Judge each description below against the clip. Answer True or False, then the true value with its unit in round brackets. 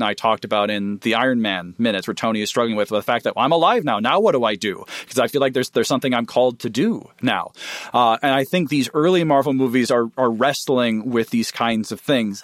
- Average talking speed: False (260 wpm)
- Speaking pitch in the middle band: False (120 Hz)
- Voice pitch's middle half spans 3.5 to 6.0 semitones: False (2.9 semitones)